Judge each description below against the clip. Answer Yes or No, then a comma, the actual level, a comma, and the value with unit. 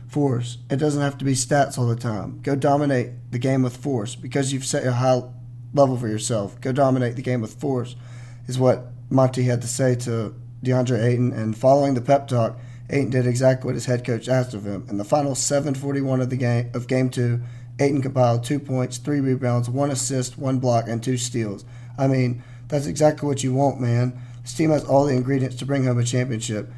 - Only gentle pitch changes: Yes, narrow, 2.0 semitones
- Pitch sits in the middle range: No, low, 125 Hz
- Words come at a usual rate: No, fast, 215 wpm